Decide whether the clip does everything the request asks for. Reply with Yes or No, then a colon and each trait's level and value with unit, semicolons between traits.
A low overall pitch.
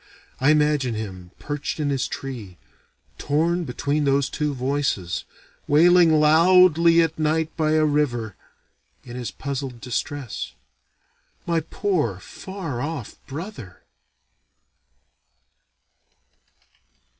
No: medium, 145 Hz